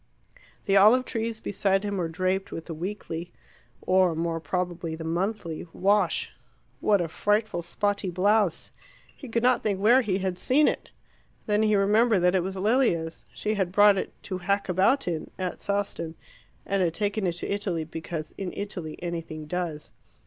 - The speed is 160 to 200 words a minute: Yes, average, 170 wpm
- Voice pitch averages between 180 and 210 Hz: Yes, high, 190 Hz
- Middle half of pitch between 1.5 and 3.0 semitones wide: No, average, 3.4 semitones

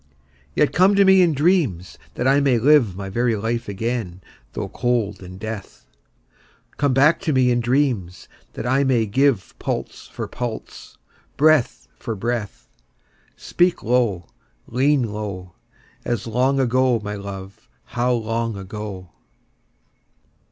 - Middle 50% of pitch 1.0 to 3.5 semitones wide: No, average, 4.7 semitones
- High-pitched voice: No, low, 120 Hz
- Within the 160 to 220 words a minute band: No, slow, 135 wpm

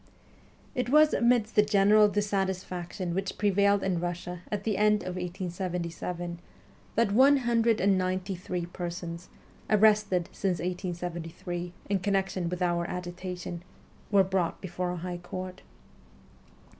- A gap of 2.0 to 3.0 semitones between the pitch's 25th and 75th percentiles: Yes, narrow, 2.6 semitones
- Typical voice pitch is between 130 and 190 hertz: Yes, medium, 185 Hz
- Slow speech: Yes, slow, 130 wpm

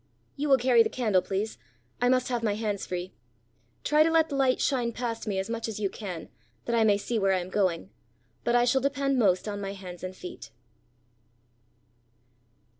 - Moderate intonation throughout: Yes, average, 4.5 semitones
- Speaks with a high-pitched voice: Yes, high, 225 Hz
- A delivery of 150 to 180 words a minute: No, average, 200 wpm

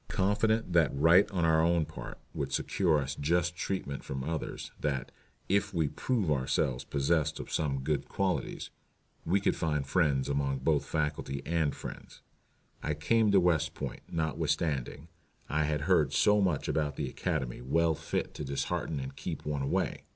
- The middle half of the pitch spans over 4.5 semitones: No, average, 3.6 semitones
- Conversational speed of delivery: Yes, average, 165 wpm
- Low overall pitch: Yes, very low, 80 Hz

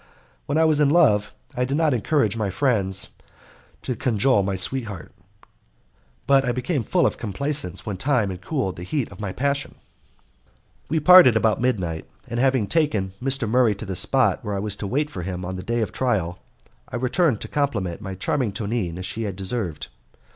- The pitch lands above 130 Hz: No, low, 115 Hz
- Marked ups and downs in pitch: Yes, wide, 5.8 semitones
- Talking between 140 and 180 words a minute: No, average, 190 wpm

